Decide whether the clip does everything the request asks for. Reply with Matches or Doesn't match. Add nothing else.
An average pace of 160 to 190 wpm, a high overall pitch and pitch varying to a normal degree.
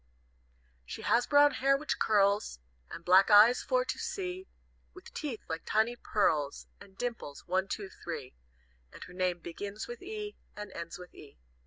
Doesn't match